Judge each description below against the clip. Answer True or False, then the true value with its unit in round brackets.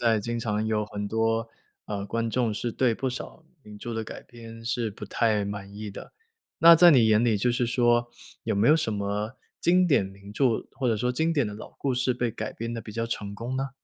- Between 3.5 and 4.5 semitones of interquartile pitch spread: False (2.7 semitones)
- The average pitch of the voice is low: True (115 Hz)